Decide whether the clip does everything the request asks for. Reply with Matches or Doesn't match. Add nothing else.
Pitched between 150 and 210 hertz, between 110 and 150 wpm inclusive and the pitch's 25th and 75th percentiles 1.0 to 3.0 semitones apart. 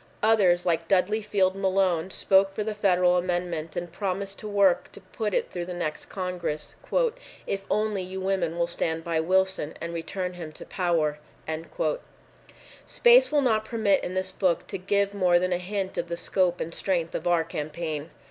Doesn't match